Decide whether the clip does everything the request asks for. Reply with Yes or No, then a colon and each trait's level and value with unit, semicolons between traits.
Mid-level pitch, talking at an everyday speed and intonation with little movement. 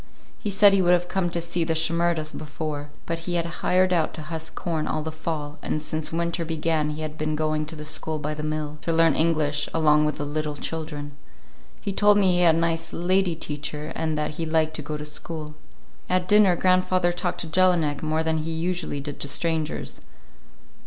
No: medium, 160 Hz; fast, 215 wpm; narrow, 2.1 semitones